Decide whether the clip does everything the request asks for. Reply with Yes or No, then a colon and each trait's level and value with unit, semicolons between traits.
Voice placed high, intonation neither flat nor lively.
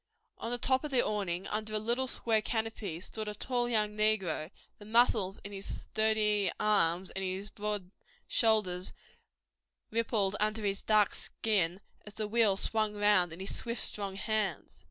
No: high, 210 Hz; narrow, 2.2 semitones